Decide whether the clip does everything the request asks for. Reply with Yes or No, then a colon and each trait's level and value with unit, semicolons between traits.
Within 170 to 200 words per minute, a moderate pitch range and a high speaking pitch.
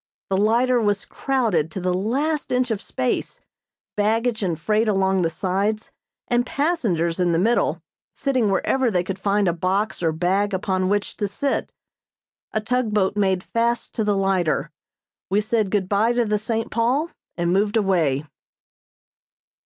No: average, 160 wpm; average, 3.7 semitones; high, 205 Hz